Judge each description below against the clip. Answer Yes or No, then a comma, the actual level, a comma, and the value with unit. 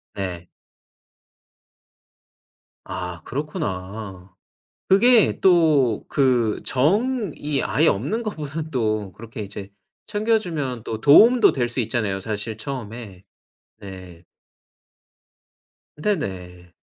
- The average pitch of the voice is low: Yes, low, 120 Hz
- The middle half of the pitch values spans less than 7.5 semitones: No, wide, 8.1 semitones